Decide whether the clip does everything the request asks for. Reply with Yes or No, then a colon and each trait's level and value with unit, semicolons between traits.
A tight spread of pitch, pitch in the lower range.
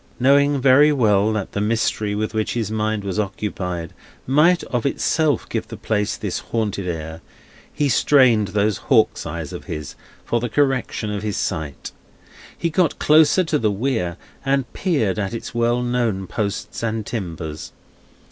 No: average, 4.8 semitones; low, 110 Hz